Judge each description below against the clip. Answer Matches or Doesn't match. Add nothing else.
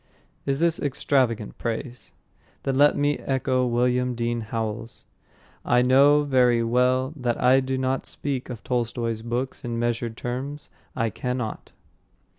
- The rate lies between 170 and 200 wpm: Doesn't match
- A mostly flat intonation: Matches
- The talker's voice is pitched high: Doesn't match